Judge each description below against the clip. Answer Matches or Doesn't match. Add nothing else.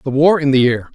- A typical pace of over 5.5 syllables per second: Matches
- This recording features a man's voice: Matches